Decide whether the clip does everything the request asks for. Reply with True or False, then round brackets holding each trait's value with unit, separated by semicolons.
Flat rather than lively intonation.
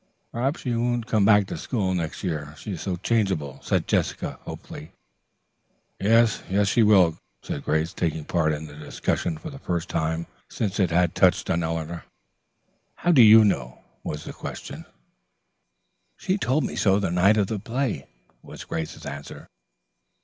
False (5.5 semitones)